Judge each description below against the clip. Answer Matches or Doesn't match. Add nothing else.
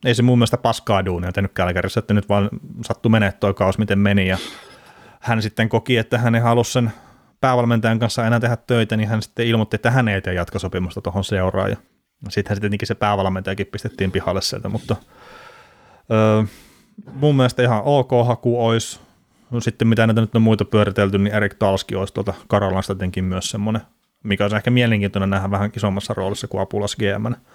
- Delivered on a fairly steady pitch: Doesn't match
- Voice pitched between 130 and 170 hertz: Doesn't match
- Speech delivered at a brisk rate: Matches